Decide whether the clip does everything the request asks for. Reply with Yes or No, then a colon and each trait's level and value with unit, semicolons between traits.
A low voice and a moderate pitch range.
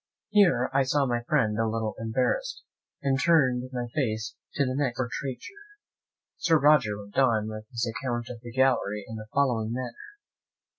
Yes: low, 125 Hz; average, 3.5 semitones